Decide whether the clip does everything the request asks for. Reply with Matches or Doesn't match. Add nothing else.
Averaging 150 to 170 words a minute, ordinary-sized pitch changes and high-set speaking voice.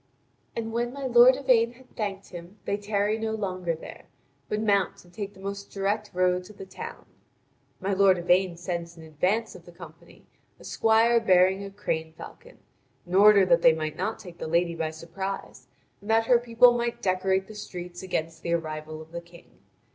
Doesn't match